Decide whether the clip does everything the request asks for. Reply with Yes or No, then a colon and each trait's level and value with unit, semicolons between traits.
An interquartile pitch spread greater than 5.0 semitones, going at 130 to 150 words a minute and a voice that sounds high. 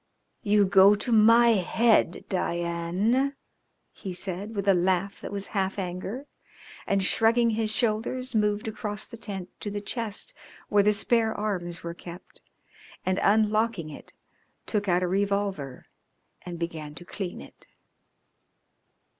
No: average, 3.3 semitones; average, 140 wpm; high, 200 Hz